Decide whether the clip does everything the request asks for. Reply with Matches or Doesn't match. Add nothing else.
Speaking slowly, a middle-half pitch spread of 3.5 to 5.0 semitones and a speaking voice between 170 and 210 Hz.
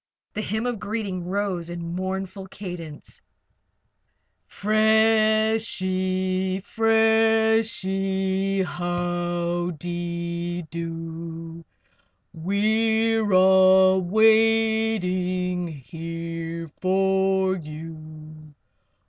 Matches